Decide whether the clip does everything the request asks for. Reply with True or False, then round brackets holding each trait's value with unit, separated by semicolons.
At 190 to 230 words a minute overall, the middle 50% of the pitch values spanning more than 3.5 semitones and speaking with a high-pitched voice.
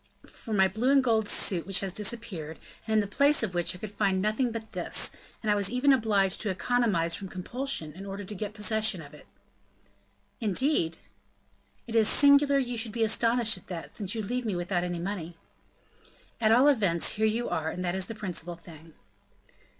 True (200 wpm; 4.2 semitones; 210 Hz)